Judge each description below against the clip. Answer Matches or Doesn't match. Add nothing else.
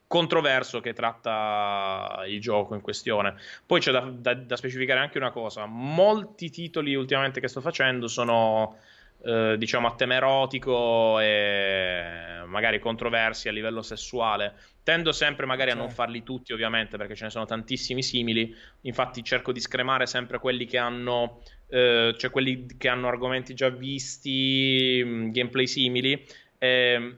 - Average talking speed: Matches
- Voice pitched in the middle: Doesn't match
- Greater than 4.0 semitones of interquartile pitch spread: Doesn't match